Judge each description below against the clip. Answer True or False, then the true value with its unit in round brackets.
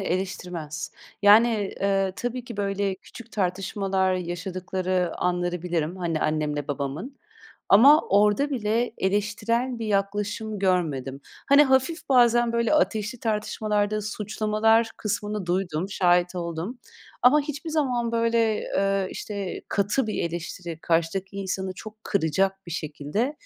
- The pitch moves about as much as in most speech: True (4.1 semitones)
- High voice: True (200 Hz)